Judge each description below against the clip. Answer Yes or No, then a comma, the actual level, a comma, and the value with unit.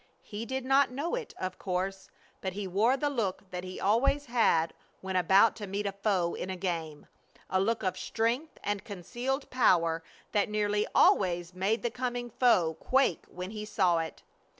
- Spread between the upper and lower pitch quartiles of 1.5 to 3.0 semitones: No, average, 4.7 semitones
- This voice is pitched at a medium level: No, high, 205 Hz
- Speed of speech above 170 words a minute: Yes, average, 180 wpm